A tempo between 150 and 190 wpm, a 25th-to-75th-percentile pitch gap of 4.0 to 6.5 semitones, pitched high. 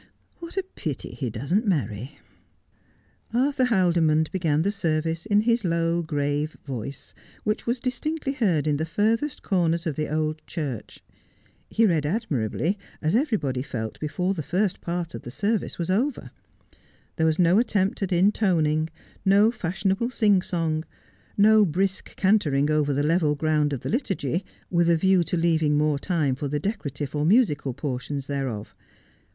No: average, 165 wpm; wide, 5.4 semitones; medium, 165 Hz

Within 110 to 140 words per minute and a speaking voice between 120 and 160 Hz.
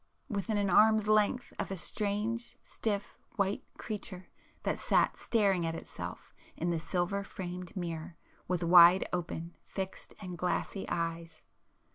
No: slow, 135 wpm; medium, 185 Hz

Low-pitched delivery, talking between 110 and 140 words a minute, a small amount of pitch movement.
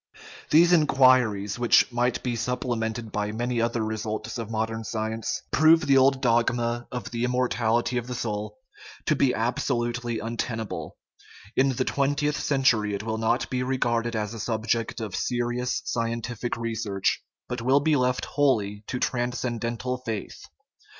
No: low, 120 Hz; average, 150 wpm; narrow, 2.1 semitones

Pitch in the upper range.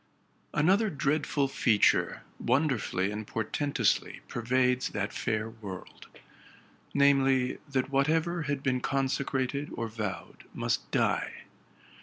No: low, 130 Hz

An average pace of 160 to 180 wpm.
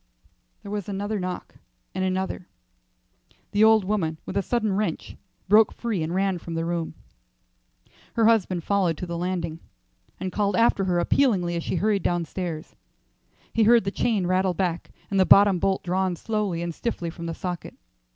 Yes: average, 170 wpm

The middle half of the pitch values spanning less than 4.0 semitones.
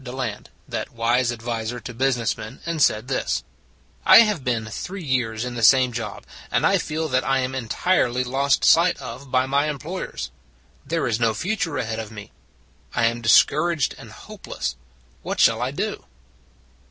Yes: average, 3.6 semitones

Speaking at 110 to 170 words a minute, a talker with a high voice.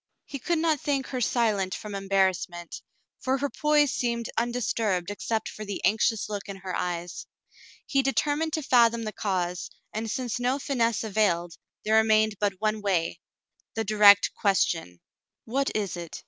Yes: average, 160 wpm; high, 215 Hz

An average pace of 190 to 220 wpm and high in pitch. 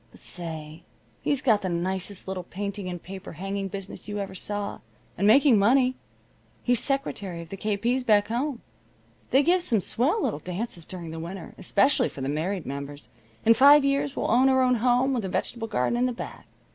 Yes: average, 195 wpm; high, 205 Hz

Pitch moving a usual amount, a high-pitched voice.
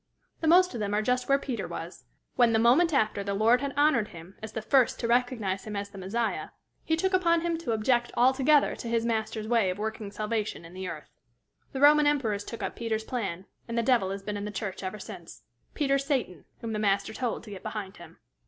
Yes: average, 4.2 semitones; high, 225 Hz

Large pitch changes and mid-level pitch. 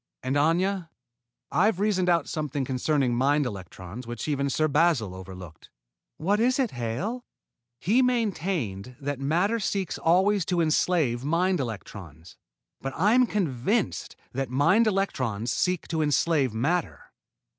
Yes: wide, 7.1 semitones; medium, 155 Hz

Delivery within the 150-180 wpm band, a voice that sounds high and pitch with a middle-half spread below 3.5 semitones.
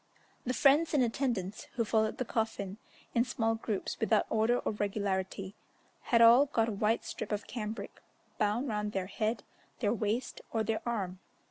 Yes: average, 165 wpm; high, 220 Hz; narrow, 2.4 semitones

